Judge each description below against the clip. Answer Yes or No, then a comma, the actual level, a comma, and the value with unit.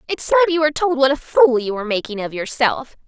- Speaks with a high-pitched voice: Yes, very high, 270 Hz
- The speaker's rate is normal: No, fast, 255 wpm